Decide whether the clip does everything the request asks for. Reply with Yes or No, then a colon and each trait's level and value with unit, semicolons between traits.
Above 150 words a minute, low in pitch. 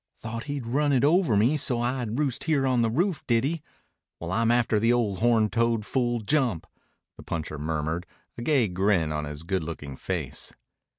Yes: average, 190 wpm; low, 115 Hz